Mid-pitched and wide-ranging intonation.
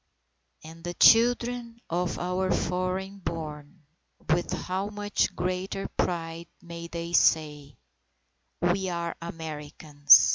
No: medium, 175 Hz; narrow, 2.6 semitones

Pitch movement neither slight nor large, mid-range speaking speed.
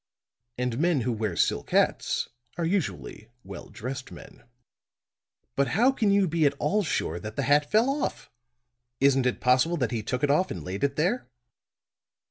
No: wide, 6.3 semitones; average, 175 wpm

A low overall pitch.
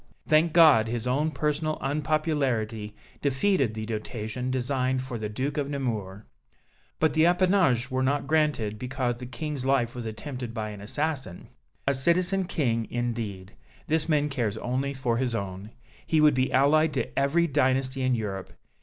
Yes: low, 130 Hz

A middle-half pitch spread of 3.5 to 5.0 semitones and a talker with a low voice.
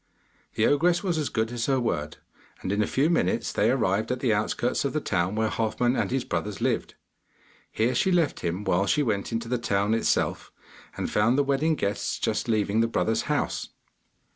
Yes: average, 4.5 semitones; low, 115 Hz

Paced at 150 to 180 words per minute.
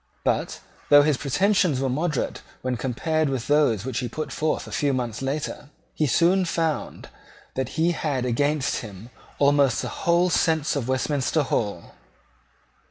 Yes: average, 155 wpm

